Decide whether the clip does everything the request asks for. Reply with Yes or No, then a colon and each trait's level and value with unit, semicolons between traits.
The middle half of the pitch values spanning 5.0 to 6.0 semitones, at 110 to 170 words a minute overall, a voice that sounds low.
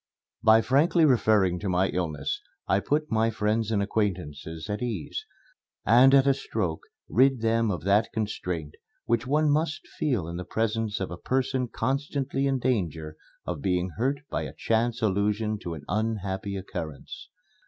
Yes: wide, 5.4 semitones; average, 160 wpm; low, 110 Hz